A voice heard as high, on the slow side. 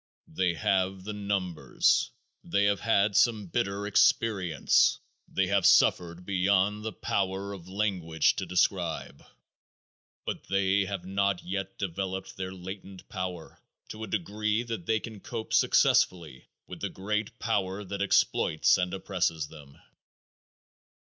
No: very low, 95 Hz; slow, 130 wpm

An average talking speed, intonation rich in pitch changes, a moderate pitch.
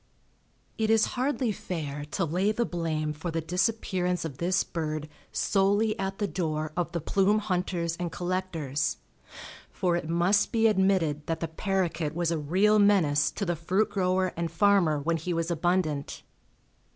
No: average, 165 wpm; average, 3.3 semitones; medium, 175 Hz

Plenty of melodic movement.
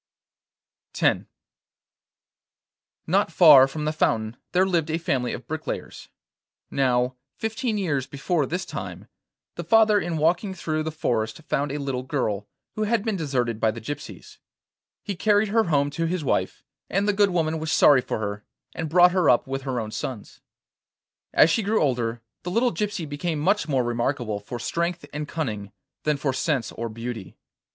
Yes: wide, 6.2 semitones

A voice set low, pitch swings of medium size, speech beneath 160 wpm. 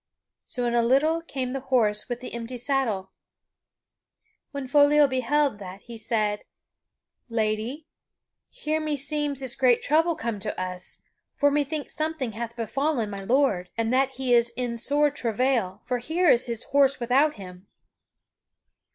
No: very high, 255 Hz; average, 4.0 semitones; average, 150 wpm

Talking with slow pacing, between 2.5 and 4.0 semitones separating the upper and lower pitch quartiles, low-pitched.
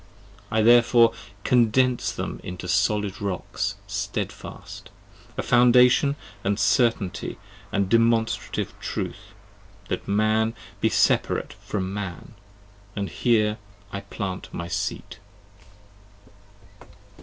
Yes: slow, 100 wpm; average, 2.9 semitones; low, 110 Hz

